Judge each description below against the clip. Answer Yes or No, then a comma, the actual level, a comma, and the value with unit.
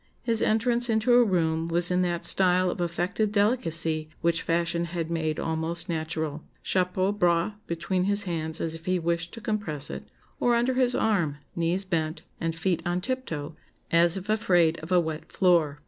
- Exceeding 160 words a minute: Yes, average, 180 wpm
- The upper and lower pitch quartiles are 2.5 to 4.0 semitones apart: Yes, average, 3.6 semitones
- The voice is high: No, medium, 175 Hz